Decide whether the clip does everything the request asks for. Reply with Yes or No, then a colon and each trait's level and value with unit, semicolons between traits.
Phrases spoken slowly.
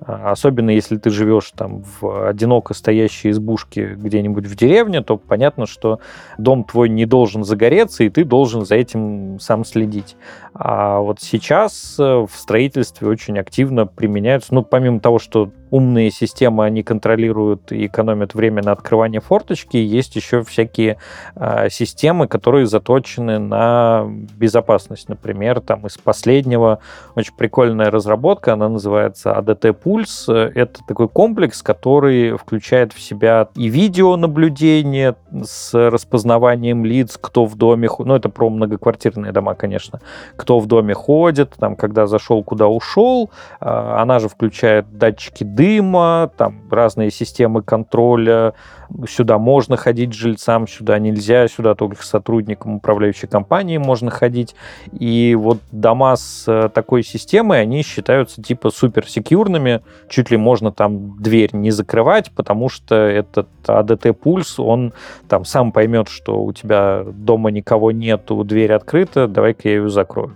No: average, 140 wpm